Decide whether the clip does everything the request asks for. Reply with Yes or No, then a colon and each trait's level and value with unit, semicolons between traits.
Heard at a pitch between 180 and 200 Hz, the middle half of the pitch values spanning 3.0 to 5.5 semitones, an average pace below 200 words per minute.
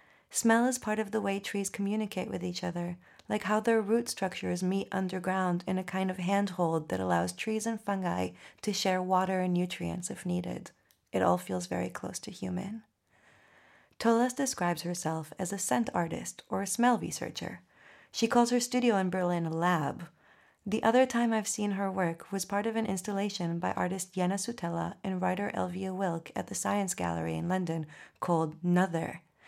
Yes: high, 190 Hz; average, 3.4 semitones; average, 180 wpm